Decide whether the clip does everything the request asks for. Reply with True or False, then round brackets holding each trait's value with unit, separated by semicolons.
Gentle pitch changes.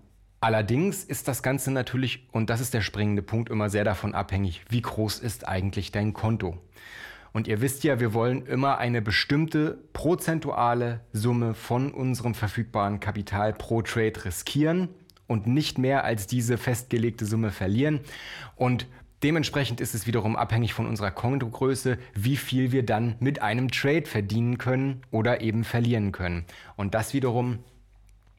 False (3.3 semitones)